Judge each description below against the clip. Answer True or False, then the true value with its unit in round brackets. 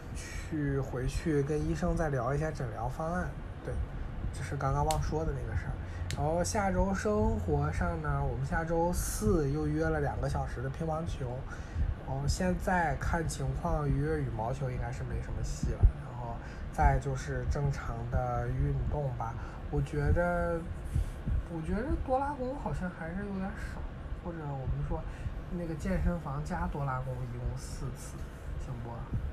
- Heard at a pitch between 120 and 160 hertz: True (140 Hz)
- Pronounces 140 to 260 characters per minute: True (235 characters per minute)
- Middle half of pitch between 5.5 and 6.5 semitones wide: True (5.9 semitones)